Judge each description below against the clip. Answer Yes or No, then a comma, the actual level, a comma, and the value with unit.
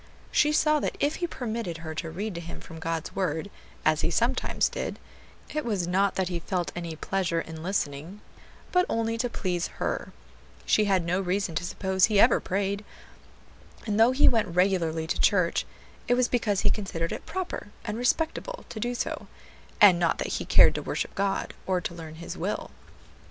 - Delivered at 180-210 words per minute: Yes, average, 190 wpm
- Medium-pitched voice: No, high, 195 Hz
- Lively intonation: No, average, 5.0 semitones